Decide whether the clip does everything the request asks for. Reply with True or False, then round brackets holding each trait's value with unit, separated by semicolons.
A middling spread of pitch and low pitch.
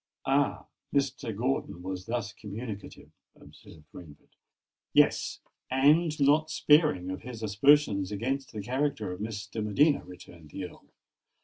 False (6.2 semitones; 115 Hz)